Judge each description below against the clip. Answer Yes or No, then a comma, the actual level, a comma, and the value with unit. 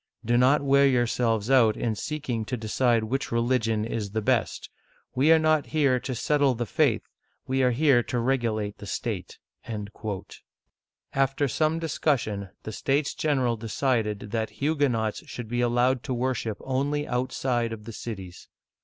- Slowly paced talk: No, average, 155 wpm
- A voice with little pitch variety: No, average, 3.3 semitones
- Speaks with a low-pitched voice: Yes, low, 125 Hz